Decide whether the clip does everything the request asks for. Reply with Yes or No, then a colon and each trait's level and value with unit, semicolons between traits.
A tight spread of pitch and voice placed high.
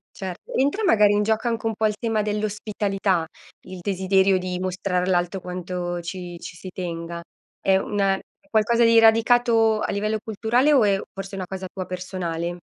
No: average, 3.2 semitones; high, 195 Hz